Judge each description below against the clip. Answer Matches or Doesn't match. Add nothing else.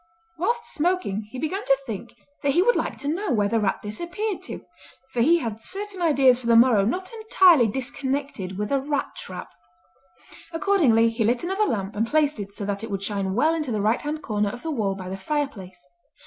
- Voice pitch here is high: Matches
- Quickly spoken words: Matches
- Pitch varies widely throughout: Matches